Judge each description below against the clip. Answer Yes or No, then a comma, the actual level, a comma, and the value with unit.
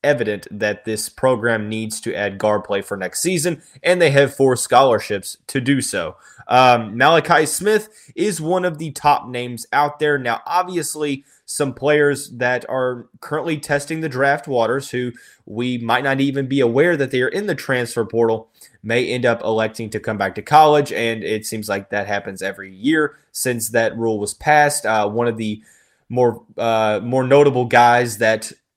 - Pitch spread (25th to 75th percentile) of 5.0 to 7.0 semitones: No, average, 4.6 semitones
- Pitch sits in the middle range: No, low, 125 Hz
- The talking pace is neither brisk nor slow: Yes, average, 185 wpm